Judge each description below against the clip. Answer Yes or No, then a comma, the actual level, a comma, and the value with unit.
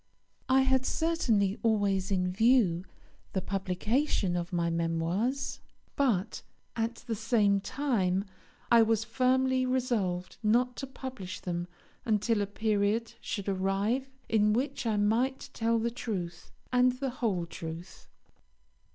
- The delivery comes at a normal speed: No, slow, 125 wpm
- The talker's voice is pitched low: No, high, 220 Hz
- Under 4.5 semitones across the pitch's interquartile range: No, average, 4.8 semitones